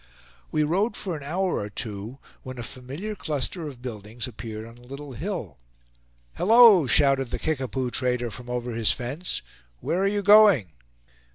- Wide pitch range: Yes, wide, 6.7 semitones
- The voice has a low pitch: Yes, low, 130 Hz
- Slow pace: No, average, 165 wpm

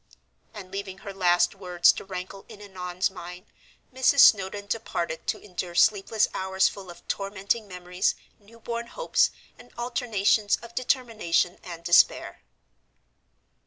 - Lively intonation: No, average, 3.2 semitones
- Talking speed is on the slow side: Yes, slow, 125 wpm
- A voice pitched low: No, high, 195 Hz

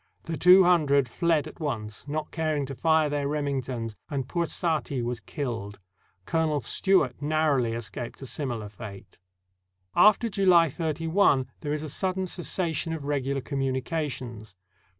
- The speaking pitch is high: No, medium, 145 Hz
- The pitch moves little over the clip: No, average, 4.4 semitones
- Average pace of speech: Yes, average, 145 wpm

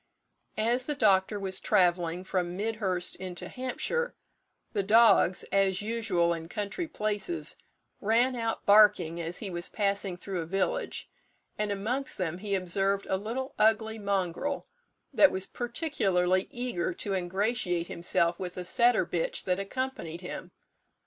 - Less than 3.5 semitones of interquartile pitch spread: No, average, 3.9 semitones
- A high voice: Yes, high, 200 Hz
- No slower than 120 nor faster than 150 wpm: Yes, average, 140 wpm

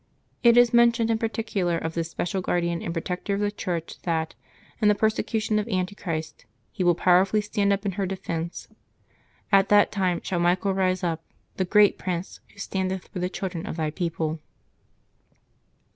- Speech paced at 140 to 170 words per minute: No, average, 180 wpm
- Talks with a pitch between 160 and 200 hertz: Yes, medium, 185 Hz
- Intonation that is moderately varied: Yes, average, 3.2 semitones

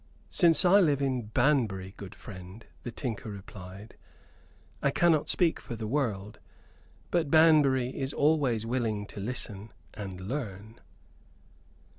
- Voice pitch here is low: Yes, low, 120 Hz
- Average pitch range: No, wide, 5.8 semitones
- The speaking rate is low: Yes, slow, 125 wpm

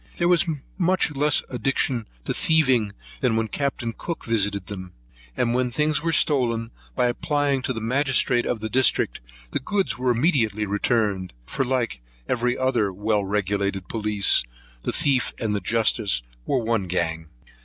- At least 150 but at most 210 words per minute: Yes, average, 155 wpm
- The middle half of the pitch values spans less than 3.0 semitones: No, average, 4.5 semitones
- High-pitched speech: No, low, 120 Hz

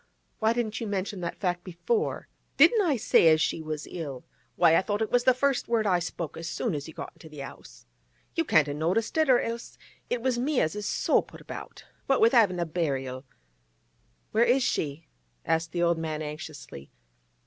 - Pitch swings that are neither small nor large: No, wide, 6.9 semitones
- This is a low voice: No, medium, 180 Hz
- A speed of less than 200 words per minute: No, fast, 205 wpm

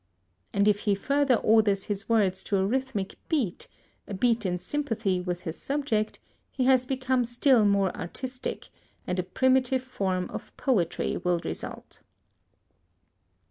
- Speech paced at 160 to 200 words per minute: No, average, 140 wpm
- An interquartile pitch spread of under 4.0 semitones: No, average, 5.3 semitones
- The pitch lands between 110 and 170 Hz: No, high, 215 Hz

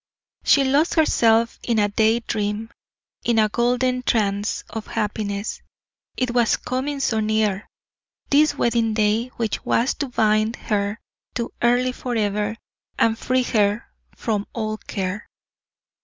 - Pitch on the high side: Yes, high, 225 Hz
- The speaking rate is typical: No, slow, 130 wpm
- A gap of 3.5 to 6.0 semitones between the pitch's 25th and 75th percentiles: No, narrow, 2.5 semitones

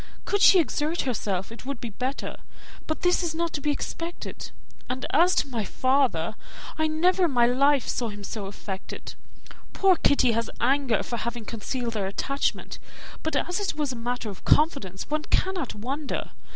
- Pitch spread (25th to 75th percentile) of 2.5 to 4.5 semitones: No, wide, 5.4 semitones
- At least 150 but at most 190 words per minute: Yes, average, 180 wpm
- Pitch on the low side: No, very high, 265 Hz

